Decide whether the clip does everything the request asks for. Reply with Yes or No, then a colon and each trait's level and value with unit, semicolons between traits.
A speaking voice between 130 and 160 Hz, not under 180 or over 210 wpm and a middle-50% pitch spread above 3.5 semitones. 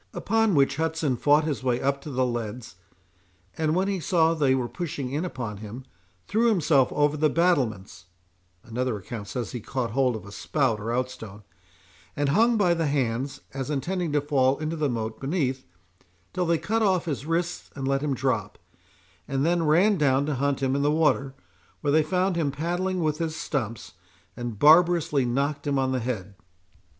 Yes: medium, 140 Hz; average, 185 wpm; average, 4.3 semitones